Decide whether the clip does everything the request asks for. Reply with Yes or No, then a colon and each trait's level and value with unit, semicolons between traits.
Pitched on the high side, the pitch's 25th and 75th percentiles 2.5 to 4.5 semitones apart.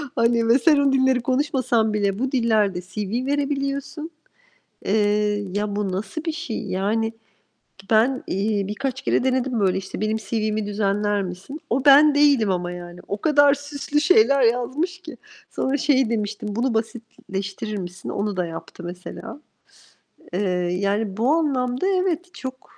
No: high, 225 Hz; average, 5.1 semitones